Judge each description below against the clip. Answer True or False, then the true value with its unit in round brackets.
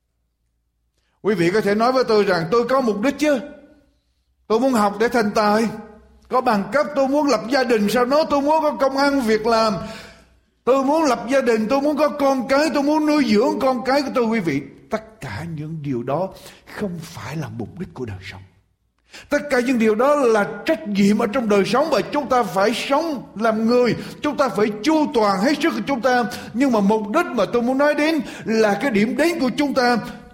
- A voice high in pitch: True (240 Hz)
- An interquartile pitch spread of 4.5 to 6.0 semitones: True (5.1 semitones)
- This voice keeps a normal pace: True (225 wpm)